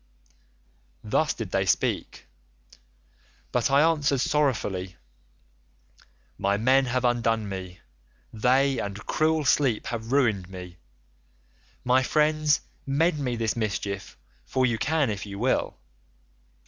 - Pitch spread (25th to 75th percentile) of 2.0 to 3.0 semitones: No, wide, 5.4 semitones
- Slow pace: Yes, slow, 115 wpm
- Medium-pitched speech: No, low, 120 Hz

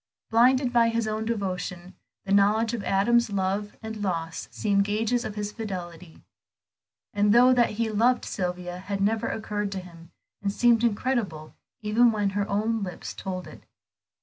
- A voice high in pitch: Yes, high, 210 Hz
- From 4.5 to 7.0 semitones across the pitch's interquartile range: No, average, 3.2 semitones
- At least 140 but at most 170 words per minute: Yes, average, 160 wpm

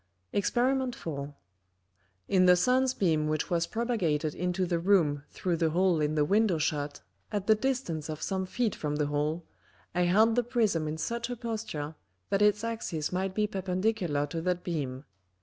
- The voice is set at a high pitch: No, medium, 180 Hz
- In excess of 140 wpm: Yes, average, 175 wpm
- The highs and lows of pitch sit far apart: Yes, wide, 5.8 semitones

